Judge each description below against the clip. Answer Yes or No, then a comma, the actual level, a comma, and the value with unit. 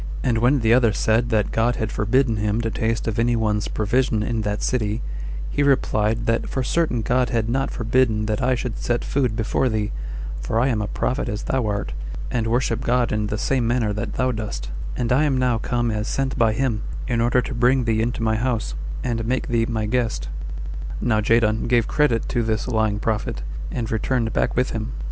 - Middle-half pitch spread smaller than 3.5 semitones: Yes, narrow, 2.4 semitones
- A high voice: No, low, 115 Hz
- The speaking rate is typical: No, fast, 210 wpm